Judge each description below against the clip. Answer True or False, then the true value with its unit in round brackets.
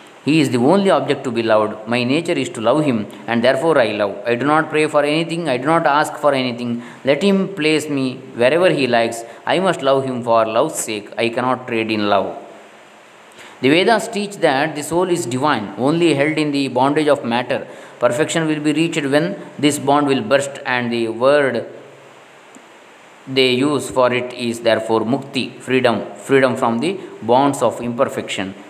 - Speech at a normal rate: False (190 wpm)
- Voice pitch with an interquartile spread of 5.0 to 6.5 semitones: False (4.1 semitones)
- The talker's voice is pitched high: False (135 Hz)